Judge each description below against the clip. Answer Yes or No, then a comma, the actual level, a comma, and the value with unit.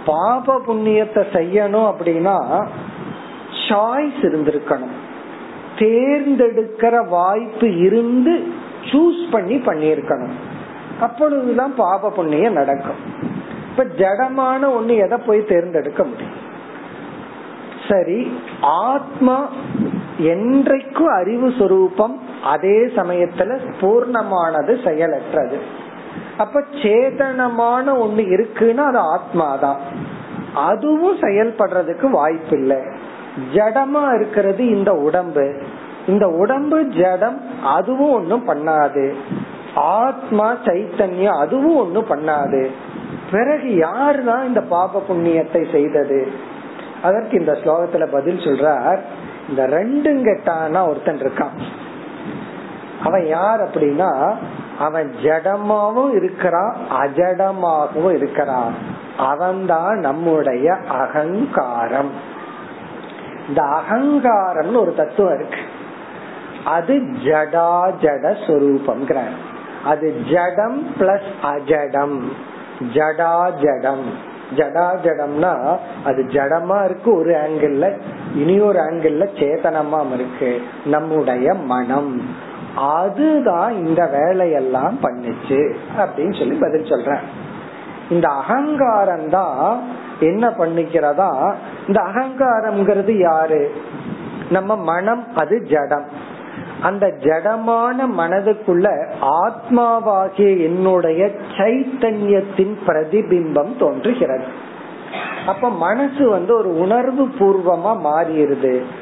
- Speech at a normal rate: No, slow, 70 wpm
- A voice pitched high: Yes, high, 195 Hz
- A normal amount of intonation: No, wide, 6.9 semitones